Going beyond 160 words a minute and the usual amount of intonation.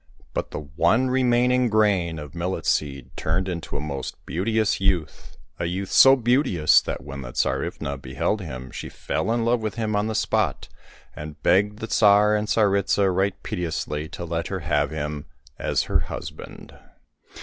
No: average, 170 wpm; wide, 5.9 semitones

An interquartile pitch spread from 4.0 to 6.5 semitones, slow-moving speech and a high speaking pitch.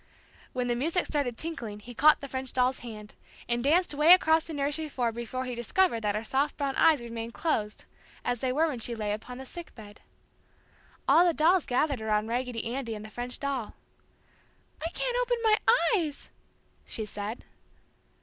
No: average, 5.1 semitones; average, 185 wpm; very high, 255 Hz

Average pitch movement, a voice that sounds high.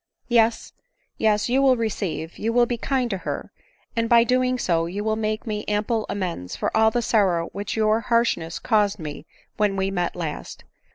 Yes: average, 3.1 semitones; high, 215 Hz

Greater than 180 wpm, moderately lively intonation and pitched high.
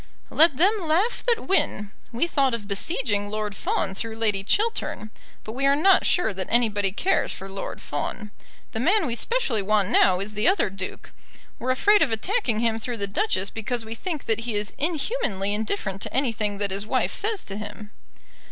No: average, 190 wpm; wide, 7.2 semitones; high, 225 Hz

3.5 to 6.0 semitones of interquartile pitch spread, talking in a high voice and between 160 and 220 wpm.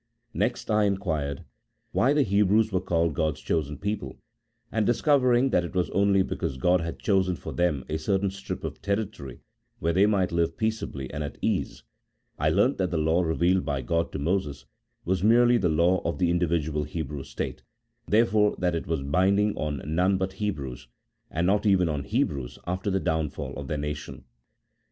No: average, 4.5 semitones; very low, 90 Hz; average, 185 wpm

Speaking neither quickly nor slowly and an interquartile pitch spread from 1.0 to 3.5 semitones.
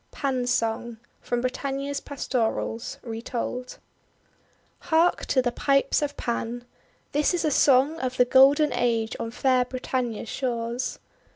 No: slow, 130 wpm; average, 2.7 semitones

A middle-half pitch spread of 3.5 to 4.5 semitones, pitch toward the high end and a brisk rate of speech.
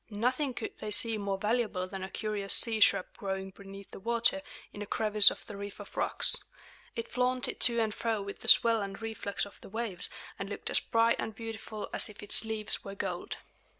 No: narrow, 2.5 semitones; high, 215 Hz; fast, 210 wpm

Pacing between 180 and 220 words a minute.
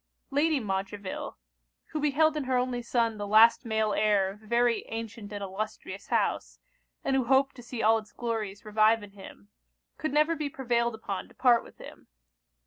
Yes: average, 185 wpm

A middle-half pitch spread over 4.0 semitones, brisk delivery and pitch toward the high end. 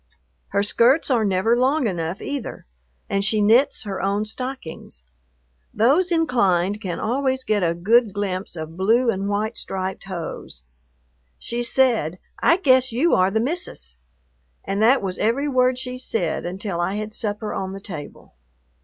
No: average, 5.1 semitones; average, 155 wpm; high, 215 Hz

